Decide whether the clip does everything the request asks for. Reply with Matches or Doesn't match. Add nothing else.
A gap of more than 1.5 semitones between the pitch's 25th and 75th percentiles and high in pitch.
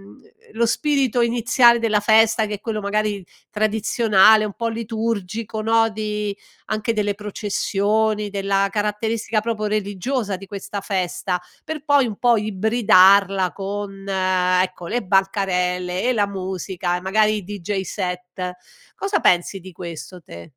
Matches